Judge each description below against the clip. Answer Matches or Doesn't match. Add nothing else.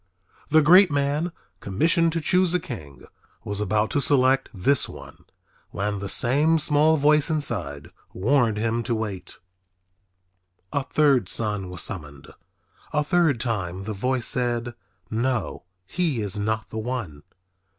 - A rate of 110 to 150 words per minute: Matches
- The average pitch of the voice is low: Matches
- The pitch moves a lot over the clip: Matches